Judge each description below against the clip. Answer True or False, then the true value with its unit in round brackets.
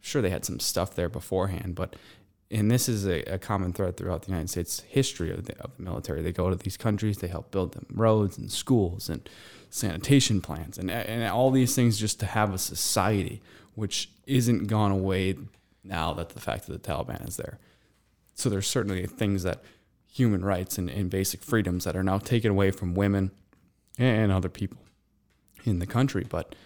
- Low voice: True (95 Hz)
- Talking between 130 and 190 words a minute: False (200 wpm)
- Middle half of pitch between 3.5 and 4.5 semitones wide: False (2.9 semitones)